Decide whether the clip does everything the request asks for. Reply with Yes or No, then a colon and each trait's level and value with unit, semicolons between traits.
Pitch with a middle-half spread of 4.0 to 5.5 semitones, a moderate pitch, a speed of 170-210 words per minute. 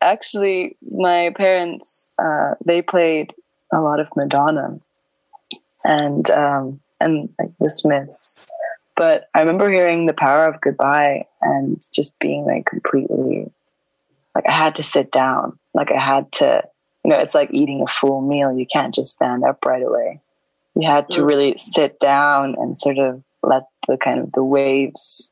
No: average, 4.8 semitones; medium, 150 Hz; average, 160 wpm